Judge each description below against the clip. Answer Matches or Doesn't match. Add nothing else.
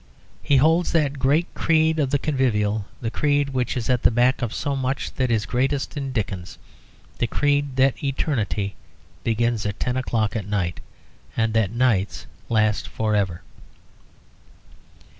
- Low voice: Matches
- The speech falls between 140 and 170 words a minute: Matches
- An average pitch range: Matches